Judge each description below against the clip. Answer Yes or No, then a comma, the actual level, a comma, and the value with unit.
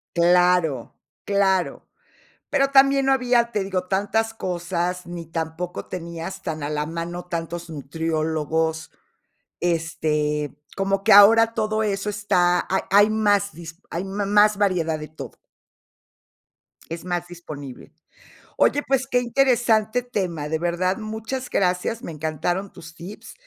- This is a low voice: No, medium, 180 Hz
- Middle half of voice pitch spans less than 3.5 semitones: No, average, 4.3 semitones